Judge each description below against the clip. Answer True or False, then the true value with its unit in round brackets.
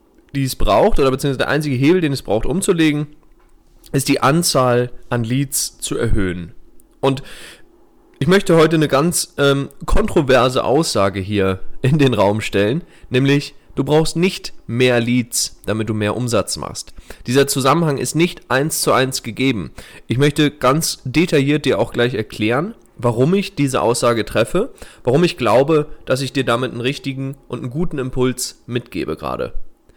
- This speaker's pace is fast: False (160 wpm)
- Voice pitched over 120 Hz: True (135 Hz)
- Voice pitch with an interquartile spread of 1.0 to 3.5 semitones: False (4.0 semitones)